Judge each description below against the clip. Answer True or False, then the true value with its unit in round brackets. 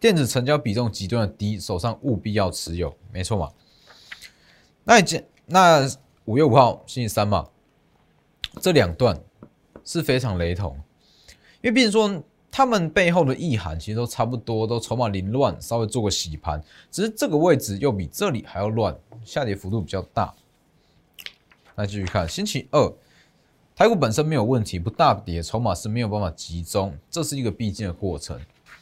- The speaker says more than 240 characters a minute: True (260 characters per minute)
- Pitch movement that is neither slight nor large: False (6.1 semitones)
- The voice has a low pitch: True (110 Hz)